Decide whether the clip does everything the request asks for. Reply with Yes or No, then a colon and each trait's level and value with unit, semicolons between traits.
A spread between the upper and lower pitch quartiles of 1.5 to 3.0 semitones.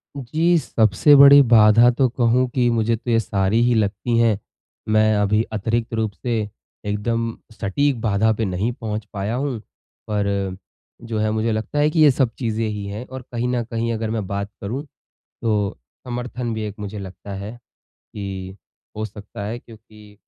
Yes: average, 2.7 semitones